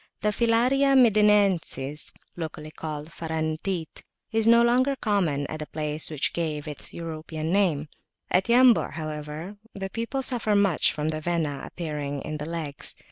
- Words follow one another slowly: No, average, 150 wpm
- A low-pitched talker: No, medium, 165 Hz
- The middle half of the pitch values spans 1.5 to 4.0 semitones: No, wide, 5.6 semitones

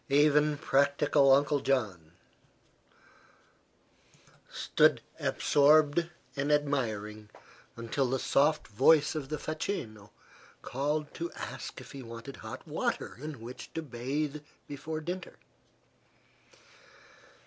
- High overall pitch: No, medium, 140 Hz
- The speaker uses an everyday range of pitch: Yes, average, 3.5 semitones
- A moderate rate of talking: No, slow, 100 wpm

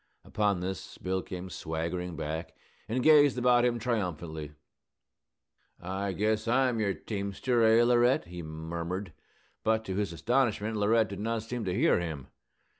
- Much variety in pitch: No, average, 4.8 semitones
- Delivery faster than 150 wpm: No, average, 145 wpm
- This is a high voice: No, low, 100 Hz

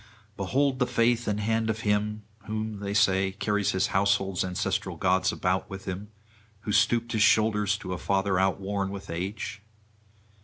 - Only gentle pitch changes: Yes, narrow, 2.1 semitones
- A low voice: Yes, low, 100 Hz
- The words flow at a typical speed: Yes, average, 160 wpm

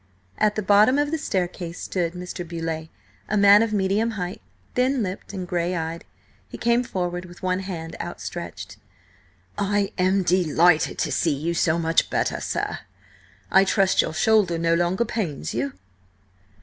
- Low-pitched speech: No, medium, 185 Hz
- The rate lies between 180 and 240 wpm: No, average, 160 wpm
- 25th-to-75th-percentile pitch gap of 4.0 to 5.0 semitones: No, average, 3.4 semitones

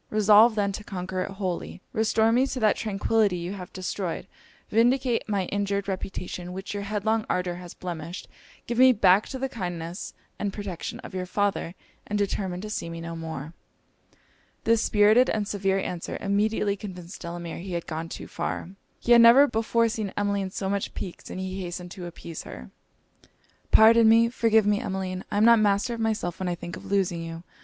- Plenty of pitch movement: No, average, 3.4 semitones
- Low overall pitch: No, high, 200 Hz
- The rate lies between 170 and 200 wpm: Yes, average, 190 wpm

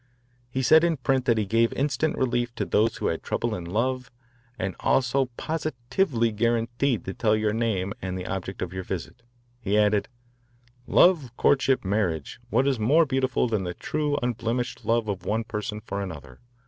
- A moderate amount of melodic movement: Yes, average, 4.4 semitones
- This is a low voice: Yes, low, 115 Hz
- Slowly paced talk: No, average, 175 wpm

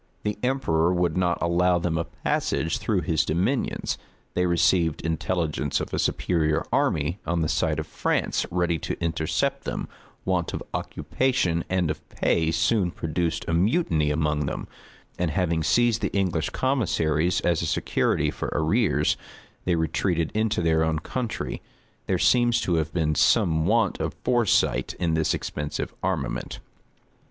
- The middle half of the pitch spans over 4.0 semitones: No, average, 2.7 semitones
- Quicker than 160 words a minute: No, average, 150 wpm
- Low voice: Yes, very low, 85 Hz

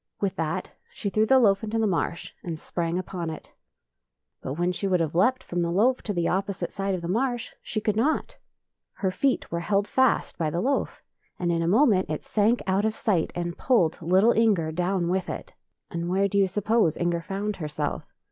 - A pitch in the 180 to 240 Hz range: Yes, high, 190 Hz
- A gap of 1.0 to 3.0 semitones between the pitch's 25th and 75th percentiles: No, average, 3.9 semitones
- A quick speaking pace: Yes, fast, 210 wpm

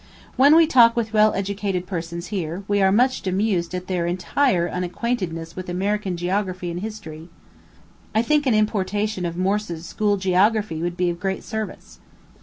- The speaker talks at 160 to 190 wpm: Yes, average, 165 wpm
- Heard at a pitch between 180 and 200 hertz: Yes, high, 190 Hz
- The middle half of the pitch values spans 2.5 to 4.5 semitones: Yes, average, 3.3 semitones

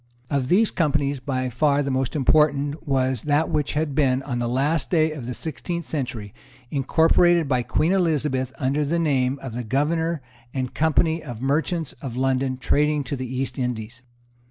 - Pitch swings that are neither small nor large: Yes, average, 3.2 semitones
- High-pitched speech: No, medium, 140 Hz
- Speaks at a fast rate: No, average, 175 wpm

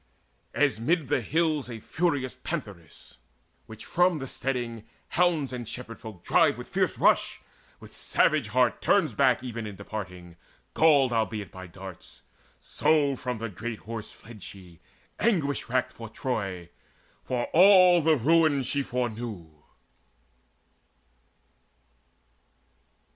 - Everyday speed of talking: No, slow, 125 wpm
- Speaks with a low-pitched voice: Yes, low, 125 Hz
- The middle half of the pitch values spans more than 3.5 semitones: Yes, wide, 5.5 semitones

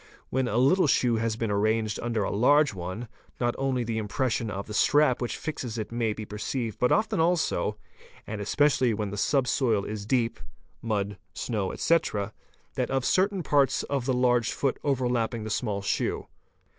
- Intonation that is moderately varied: Yes, average, 3.8 semitones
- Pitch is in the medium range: No, low, 120 Hz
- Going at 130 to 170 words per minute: No, average, 180 wpm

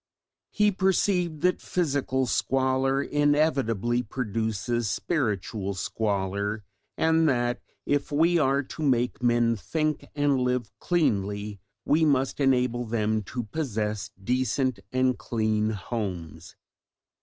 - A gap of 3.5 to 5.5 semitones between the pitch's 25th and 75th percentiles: Yes, average, 5.0 semitones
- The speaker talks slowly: Yes, slow, 110 wpm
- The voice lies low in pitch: Yes, low, 125 Hz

